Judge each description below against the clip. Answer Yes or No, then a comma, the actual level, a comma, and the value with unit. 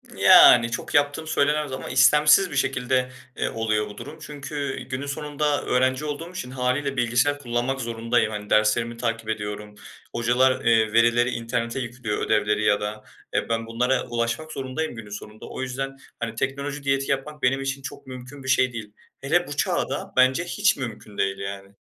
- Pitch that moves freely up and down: No, average, 3.4 semitones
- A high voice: No, low, 125 Hz